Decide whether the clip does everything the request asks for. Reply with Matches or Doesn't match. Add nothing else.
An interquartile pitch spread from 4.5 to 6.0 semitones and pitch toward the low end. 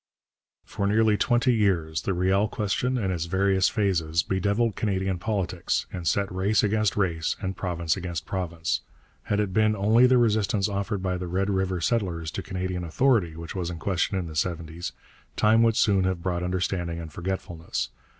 Doesn't match